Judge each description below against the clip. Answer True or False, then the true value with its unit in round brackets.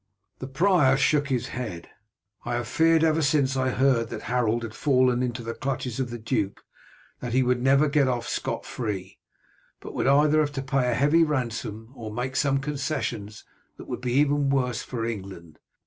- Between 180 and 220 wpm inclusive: True (190 wpm)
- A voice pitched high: False (130 Hz)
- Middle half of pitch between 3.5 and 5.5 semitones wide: False (3.1 semitones)